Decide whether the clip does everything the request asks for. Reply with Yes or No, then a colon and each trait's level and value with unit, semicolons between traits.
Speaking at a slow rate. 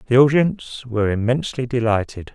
Yes: slow, 130 wpm